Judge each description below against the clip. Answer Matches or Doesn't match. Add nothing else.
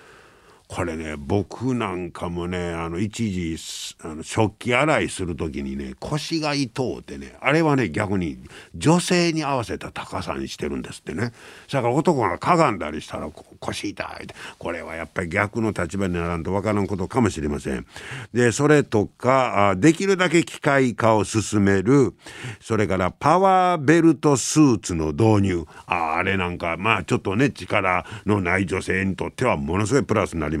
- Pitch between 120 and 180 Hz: Doesn't match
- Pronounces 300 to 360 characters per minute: Matches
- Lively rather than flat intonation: Matches